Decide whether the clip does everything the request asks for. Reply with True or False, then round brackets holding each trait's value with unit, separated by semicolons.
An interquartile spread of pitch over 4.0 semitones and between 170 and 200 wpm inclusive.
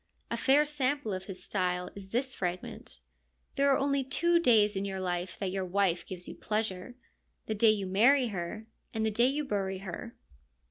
True (5.5 semitones; 195 wpm)